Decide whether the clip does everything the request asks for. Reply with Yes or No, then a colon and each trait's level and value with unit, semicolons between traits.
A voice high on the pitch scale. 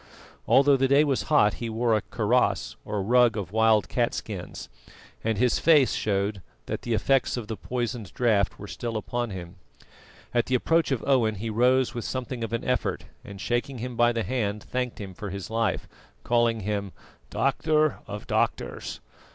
No: low, 115 Hz